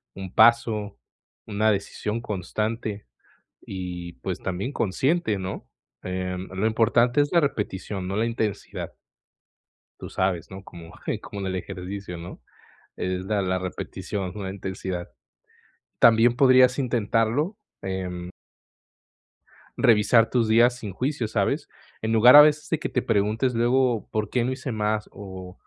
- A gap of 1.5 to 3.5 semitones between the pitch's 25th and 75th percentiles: No, average, 4.1 semitones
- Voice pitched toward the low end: Yes, low, 105 Hz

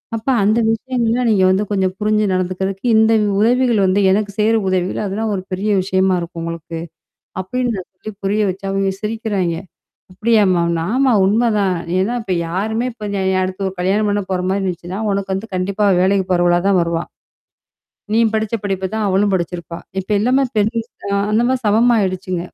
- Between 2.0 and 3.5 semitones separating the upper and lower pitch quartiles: Yes, average, 2.9 semitones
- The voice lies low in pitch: No, high, 195 Hz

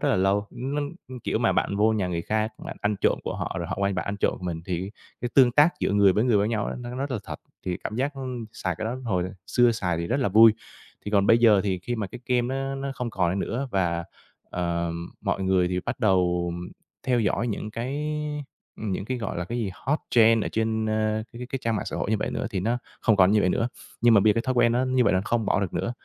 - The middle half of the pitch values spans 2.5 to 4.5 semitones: Yes, average, 4.2 semitones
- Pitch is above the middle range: No, low, 110 Hz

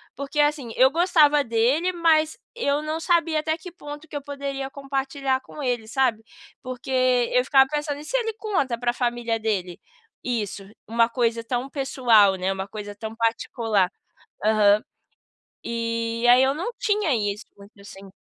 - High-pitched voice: Yes, very high, 260 Hz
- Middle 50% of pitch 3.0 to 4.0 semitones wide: No, average, 4.6 semitones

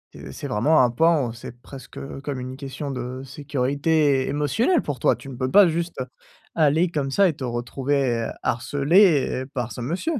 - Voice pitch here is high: No, medium, 140 Hz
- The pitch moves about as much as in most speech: Yes, average, 3.6 semitones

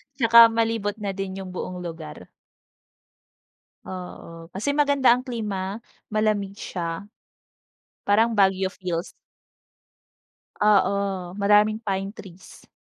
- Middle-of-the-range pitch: No, high, 200 Hz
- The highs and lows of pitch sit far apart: No, narrow, 2.4 semitones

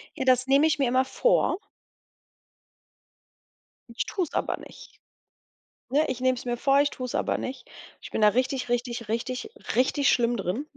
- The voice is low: No, very high, 255 Hz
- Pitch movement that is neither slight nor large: No, narrow, 2.3 semitones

